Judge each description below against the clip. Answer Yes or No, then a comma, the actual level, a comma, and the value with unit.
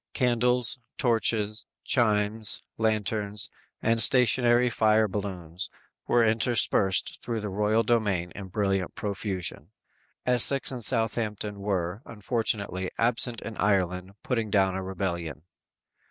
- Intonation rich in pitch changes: No, average, 3.0 semitones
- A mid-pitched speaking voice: No, low, 105 Hz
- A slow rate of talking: Yes, slow, 110 wpm